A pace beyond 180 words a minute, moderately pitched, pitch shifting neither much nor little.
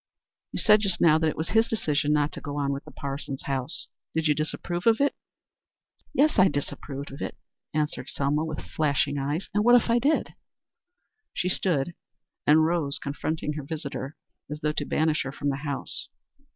Yes: average, 190 wpm; medium, 150 Hz; average, 3.4 semitones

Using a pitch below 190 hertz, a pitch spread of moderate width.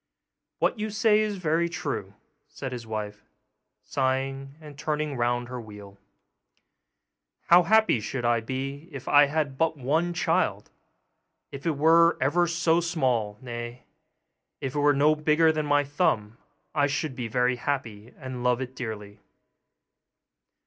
Yes: medium, 140 Hz; average, 4.6 semitones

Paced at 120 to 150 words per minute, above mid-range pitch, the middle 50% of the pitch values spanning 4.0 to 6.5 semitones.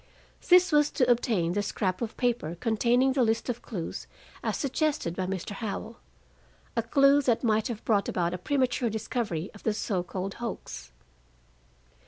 No: average, 165 wpm; high, 225 Hz; average, 4.5 semitones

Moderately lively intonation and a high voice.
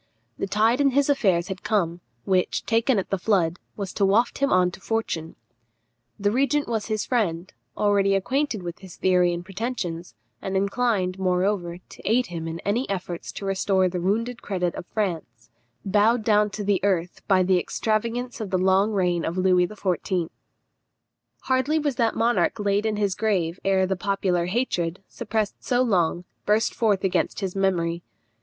Yes: average, 3.5 semitones; high, 195 Hz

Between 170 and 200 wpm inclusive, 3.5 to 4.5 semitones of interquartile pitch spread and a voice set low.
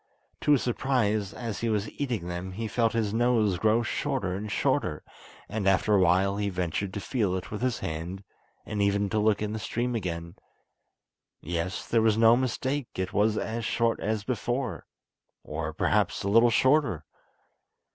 Yes: average, 175 wpm; average, 3.8 semitones; low, 105 Hz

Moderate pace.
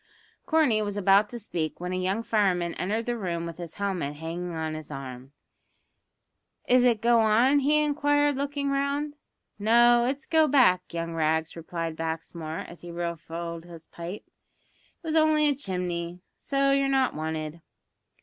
Yes: average, 160 wpm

